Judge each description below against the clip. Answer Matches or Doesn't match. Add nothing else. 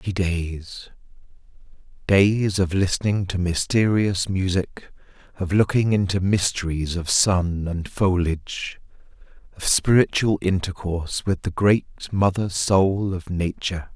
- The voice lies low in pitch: Matches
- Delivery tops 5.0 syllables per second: Doesn't match